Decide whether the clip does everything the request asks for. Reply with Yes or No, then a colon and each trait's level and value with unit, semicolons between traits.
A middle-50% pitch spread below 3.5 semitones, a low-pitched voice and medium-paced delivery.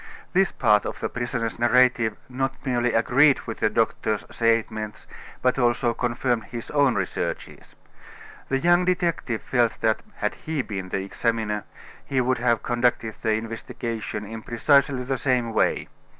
Yes: narrow, 2.6 semitones; low, 120 Hz; average, 150 wpm